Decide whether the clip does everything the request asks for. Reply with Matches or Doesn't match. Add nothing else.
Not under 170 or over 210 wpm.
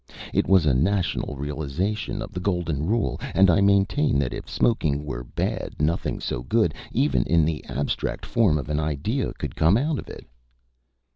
Matches